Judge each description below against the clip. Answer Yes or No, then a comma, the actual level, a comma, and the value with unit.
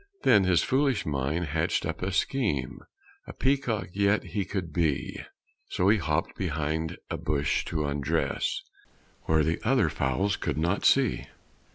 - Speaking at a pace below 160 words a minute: Yes, average, 150 wpm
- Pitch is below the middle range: Yes, very low, 85 Hz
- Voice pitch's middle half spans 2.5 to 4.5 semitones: No, average, 5.0 semitones